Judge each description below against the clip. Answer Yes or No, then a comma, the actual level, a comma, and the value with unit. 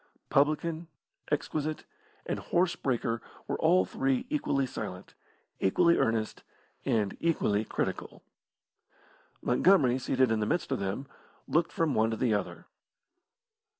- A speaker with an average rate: No, slow, 120 wpm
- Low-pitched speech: Yes, low, 130 Hz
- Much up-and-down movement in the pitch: Yes, wide, 5.8 semitones